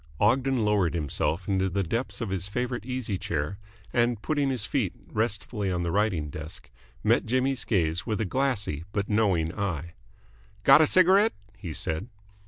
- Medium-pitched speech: No, low, 105 Hz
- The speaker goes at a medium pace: Yes, average, 165 wpm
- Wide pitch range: Yes, wide, 5.9 semitones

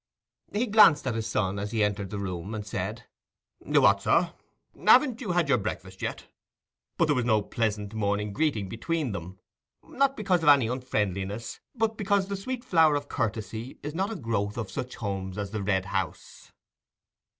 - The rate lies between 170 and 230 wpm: Yes, average, 180 wpm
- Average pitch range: No, wide, 8.6 semitones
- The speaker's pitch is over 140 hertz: No, low, 115 Hz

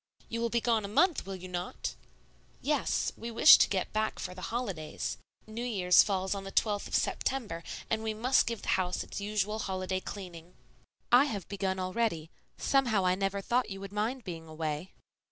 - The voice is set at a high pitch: Yes, high, 200 Hz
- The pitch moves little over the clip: No, average, 3.8 semitones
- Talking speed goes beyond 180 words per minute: Yes, average, 190 wpm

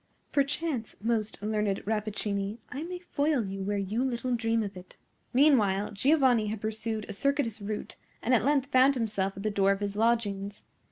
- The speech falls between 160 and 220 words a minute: Yes, average, 175 wpm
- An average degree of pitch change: Yes, average, 4.1 semitones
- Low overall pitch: No, high, 220 Hz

